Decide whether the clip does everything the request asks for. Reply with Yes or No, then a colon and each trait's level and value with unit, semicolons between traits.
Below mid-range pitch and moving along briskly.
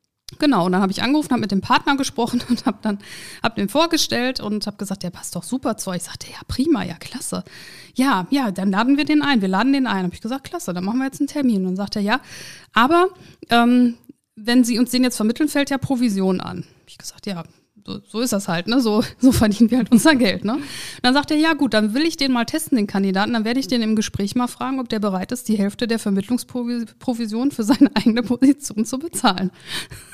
No: high, 240 Hz; fast, 245 wpm